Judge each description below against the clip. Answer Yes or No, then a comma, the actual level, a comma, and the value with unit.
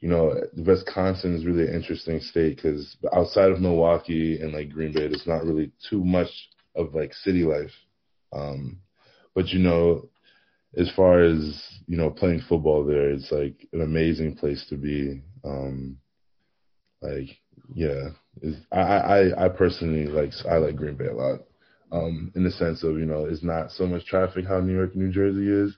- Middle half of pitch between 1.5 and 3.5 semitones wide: Yes, average, 3.1 semitones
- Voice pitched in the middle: No, very low, 80 Hz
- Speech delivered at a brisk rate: No, average, 175 wpm